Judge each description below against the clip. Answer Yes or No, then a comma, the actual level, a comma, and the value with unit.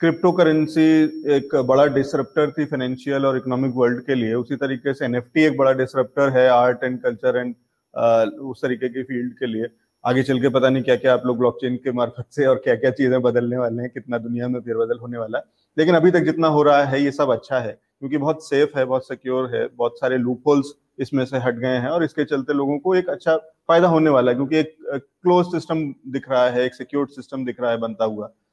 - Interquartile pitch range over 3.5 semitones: No, average, 3.0 semitones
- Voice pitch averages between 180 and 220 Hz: No, low, 130 Hz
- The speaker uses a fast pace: Yes, fast, 230 wpm